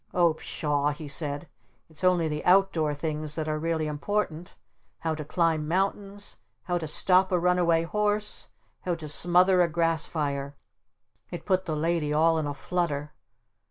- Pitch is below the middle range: No, medium, 165 Hz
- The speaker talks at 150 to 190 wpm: Yes, average, 160 wpm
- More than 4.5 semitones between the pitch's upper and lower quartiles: No, average, 3.0 semitones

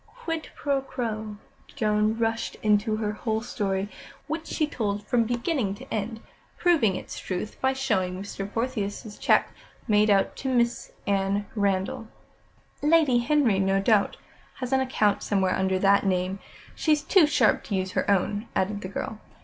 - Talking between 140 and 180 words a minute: Yes, average, 155 wpm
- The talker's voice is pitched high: Yes, high, 215 Hz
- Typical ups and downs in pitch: Yes, average, 4.2 semitones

